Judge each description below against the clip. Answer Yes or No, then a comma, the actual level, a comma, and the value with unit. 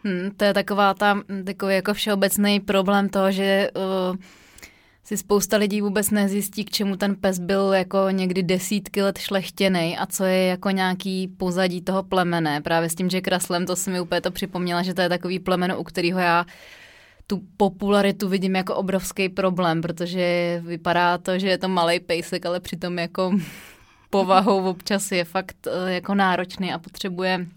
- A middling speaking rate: No, fast, 175 wpm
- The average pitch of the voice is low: No, high, 190 Hz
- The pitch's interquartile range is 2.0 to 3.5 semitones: No, narrow, 1.6 semitones